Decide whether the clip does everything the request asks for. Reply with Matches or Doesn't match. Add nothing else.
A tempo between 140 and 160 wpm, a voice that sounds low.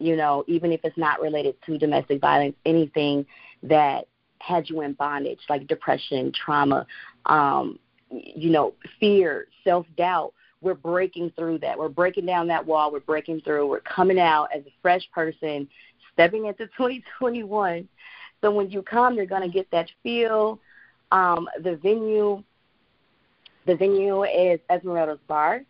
Doesn't match